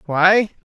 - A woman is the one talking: No, male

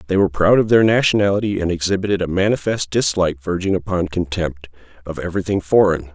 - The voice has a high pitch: No, very low, 90 Hz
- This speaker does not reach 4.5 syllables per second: No, 6.5 syllables/s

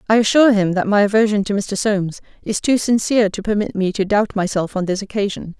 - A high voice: Yes, high, 205 Hz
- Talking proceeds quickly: Yes, fast, 225 wpm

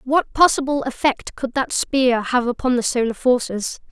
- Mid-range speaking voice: No, very high, 255 Hz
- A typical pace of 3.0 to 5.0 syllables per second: Yes, 4.6 syllables/s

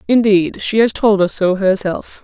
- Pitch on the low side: No, high, 200 Hz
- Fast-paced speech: No, average, 190 wpm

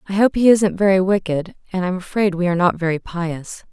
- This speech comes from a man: No, female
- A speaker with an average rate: No, fast, 225 wpm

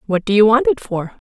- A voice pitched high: Yes, high, 220 Hz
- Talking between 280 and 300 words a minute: Yes, fast, 285 wpm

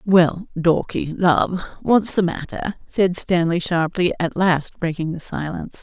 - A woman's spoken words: Yes, female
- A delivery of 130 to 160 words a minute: Yes, average, 145 wpm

